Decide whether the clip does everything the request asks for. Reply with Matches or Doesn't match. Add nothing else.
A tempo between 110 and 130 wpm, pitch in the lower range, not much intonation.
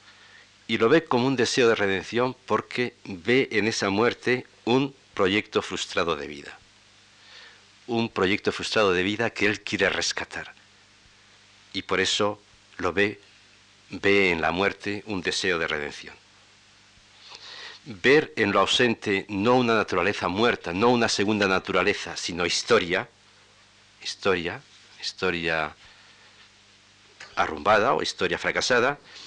Matches